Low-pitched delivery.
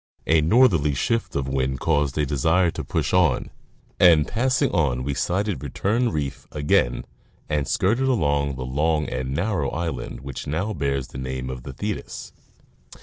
Yes: very low, 75 Hz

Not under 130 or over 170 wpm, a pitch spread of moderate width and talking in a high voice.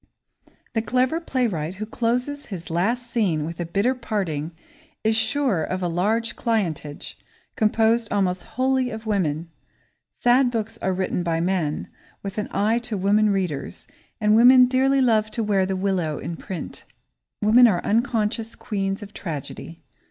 Yes: average, 150 wpm; average, 4.5 semitones; high, 210 Hz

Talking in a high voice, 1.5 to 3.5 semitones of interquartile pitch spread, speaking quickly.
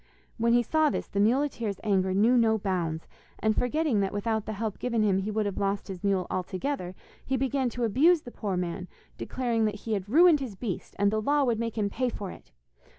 No: high, 220 Hz; average, 3.9 semitones; fast, 220 wpm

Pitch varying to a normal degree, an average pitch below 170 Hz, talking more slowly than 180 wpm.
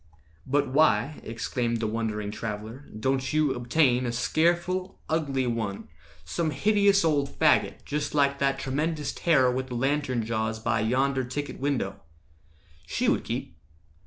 Yes: average, 4.2 semitones; low, 135 Hz; average, 140 wpm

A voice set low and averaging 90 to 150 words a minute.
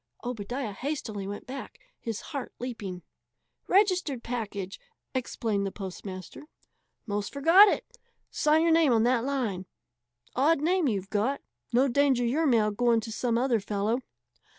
No: high, 240 Hz; average, 140 wpm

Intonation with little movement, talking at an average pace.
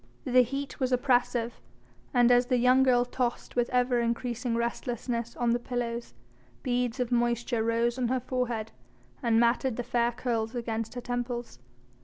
Yes: narrow, 1.1 semitones; average, 160 wpm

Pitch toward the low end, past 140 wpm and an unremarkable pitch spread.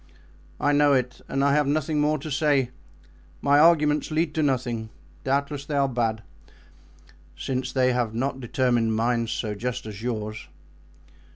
Yes: low, 130 Hz; average, 155 wpm; average, 3.6 semitones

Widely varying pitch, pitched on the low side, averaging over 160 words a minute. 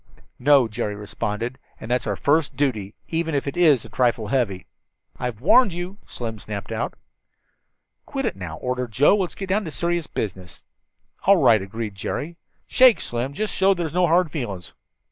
Yes: wide, 7.9 semitones; low, 130 Hz; average, 180 wpm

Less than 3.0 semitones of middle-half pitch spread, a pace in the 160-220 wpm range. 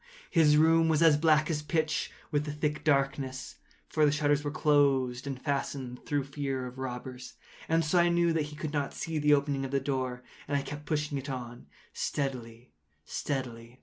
Yes: narrow, 2.5 semitones; average, 185 wpm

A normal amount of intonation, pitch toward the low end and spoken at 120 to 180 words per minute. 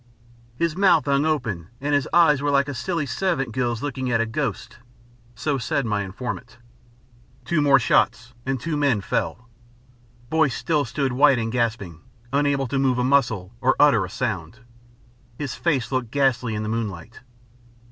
Yes: average, 4.0 semitones; low, 130 Hz; average, 165 wpm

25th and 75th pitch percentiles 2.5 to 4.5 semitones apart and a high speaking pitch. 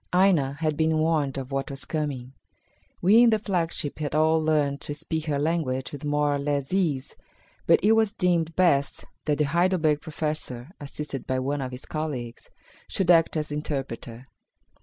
No: average, 2.8 semitones; medium, 150 Hz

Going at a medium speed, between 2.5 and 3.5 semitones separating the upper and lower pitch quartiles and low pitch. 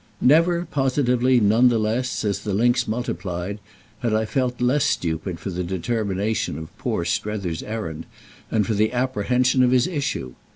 No: average, 165 wpm; average, 4.4 semitones; low, 110 Hz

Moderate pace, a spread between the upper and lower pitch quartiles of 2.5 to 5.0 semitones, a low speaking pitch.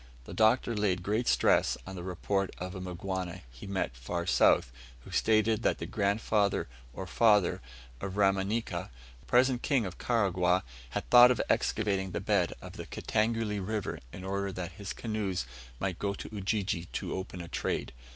Yes: average, 170 wpm; average, 2.8 semitones; low, 100 Hz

